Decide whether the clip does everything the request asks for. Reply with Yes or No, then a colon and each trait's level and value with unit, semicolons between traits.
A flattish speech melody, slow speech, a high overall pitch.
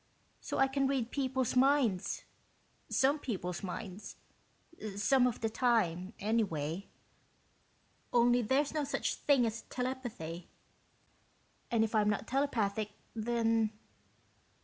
No: average, 4.3 semitones; slow, 110 wpm; high, 230 Hz